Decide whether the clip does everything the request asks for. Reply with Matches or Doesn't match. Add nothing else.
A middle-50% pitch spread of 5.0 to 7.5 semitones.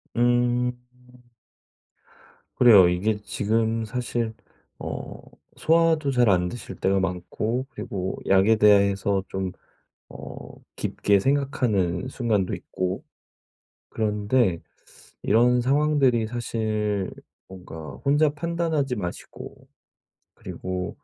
Doesn't match